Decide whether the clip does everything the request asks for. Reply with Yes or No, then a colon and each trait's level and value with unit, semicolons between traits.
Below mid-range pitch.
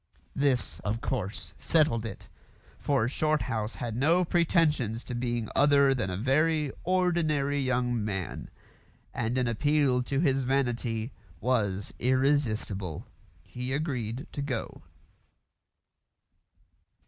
Yes: low, 130 Hz